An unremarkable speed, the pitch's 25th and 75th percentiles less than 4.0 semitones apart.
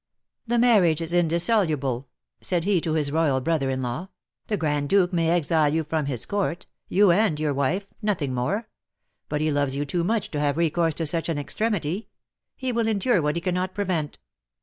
No: average, 195 wpm; average, 4.5 semitones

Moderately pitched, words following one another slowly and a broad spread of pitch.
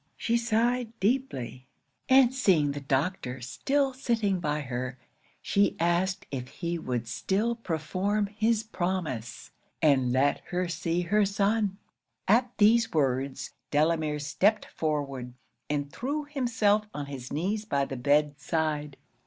Yes: medium, 170 Hz; slow, 130 wpm; wide, 7.4 semitones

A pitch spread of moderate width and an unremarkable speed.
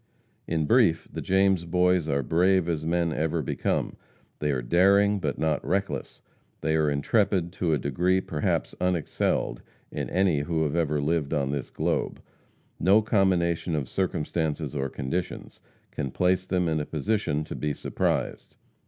Yes: average, 3.6 semitones; average, 155 wpm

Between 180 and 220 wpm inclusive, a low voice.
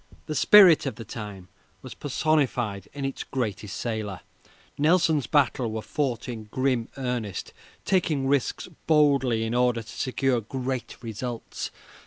No: slow, 135 wpm; low, 125 Hz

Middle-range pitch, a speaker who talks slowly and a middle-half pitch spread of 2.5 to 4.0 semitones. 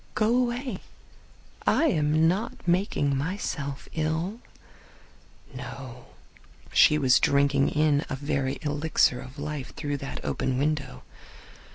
Yes: medium, 145 Hz; slow, 110 wpm; average, 2.9 semitones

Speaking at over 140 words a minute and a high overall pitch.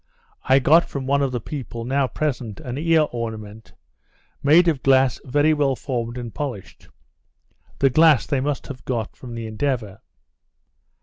No: average, 160 wpm; low, 130 Hz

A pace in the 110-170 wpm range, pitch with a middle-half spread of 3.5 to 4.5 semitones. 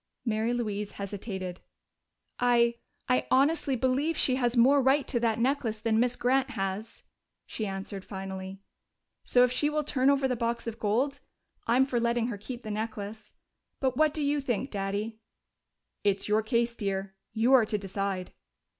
Yes: average, 165 wpm; average, 3.9 semitones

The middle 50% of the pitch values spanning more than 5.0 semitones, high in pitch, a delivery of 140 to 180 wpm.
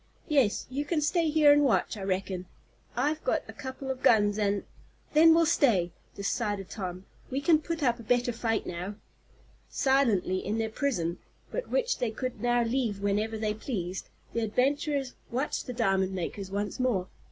Yes: wide, 5.6 semitones; high, 230 Hz; average, 175 wpm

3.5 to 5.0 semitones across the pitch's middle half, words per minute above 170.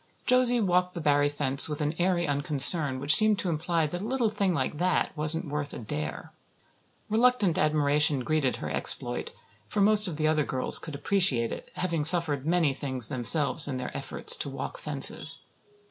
Yes: average, 4.0 semitones; average, 180 wpm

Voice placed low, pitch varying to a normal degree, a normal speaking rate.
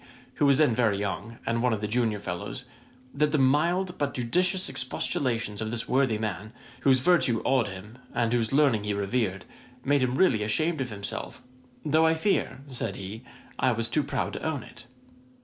Yes: low, 120 Hz; average, 4.7 semitones; average, 185 wpm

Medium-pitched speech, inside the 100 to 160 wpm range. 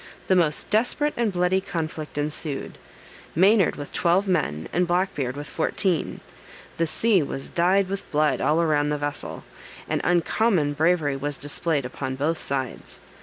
Yes: medium, 160 Hz; average, 155 wpm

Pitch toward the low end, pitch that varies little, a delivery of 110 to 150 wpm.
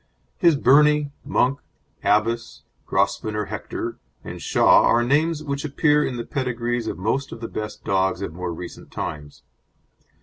No: low, 120 Hz; average, 5.1 semitones; average, 145 wpm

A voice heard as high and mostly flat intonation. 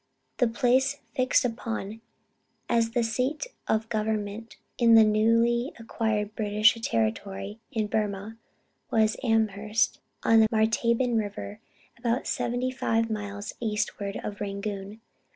Yes: high, 220 Hz; narrow, 1.9 semitones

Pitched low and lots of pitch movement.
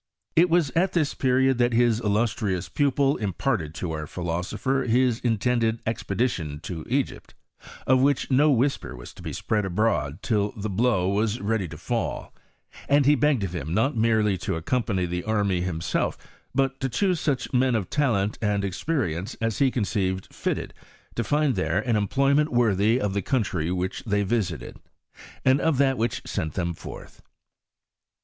Yes: low, 110 Hz; wide, 5.7 semitones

